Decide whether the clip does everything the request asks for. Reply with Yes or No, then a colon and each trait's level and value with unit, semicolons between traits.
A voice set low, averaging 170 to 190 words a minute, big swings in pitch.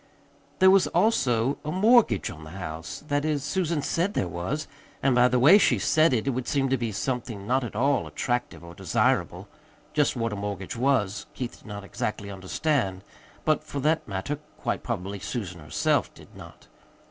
Yes: low, 125 Hz; average, 185 wpm; wide, 6.7 semitones